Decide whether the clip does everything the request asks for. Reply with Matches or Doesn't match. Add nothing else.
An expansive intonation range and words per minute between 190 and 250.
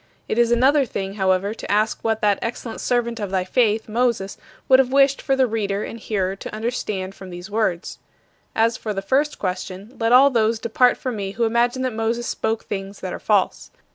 Doesn't match